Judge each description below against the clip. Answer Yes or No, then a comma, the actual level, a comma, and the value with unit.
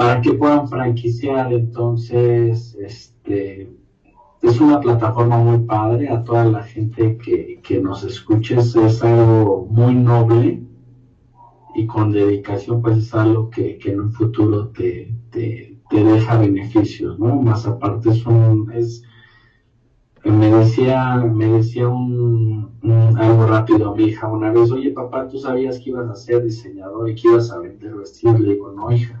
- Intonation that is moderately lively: No, narrow, 1.5 semitones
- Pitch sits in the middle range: No, low, 115 Hz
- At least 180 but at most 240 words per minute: No, average, 155 wpm